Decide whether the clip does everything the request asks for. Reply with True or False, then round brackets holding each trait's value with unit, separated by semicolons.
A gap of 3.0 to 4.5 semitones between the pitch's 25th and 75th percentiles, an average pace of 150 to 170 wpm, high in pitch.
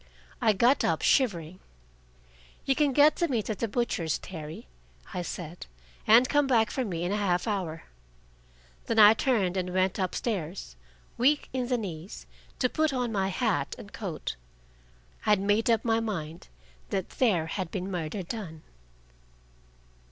False (5.0 semitones; 160 wpm; 205 Hz)